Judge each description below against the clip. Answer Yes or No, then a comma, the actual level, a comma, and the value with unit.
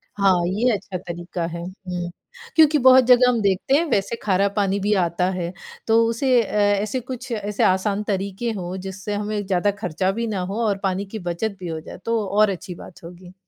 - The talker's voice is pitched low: No, high, 200 Hz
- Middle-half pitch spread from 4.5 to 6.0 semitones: No, average, 3.3 semitones